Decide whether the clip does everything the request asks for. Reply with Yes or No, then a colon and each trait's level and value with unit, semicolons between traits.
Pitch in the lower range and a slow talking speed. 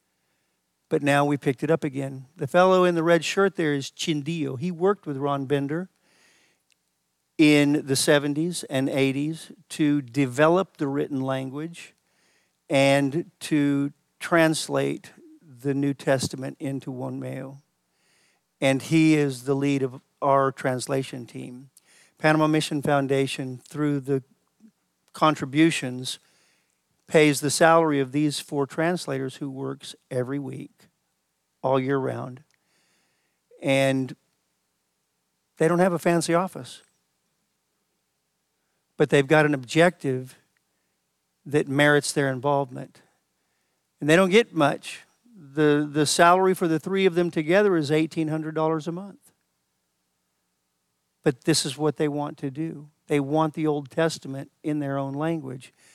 No: medium, 145 Hz; slow, 130 wpm